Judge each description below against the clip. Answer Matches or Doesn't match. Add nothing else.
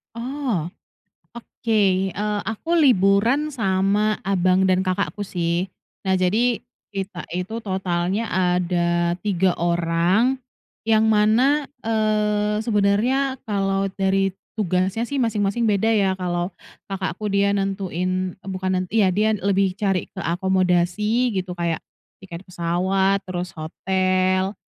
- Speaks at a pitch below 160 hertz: Doesn't match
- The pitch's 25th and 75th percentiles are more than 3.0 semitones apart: Doesn't match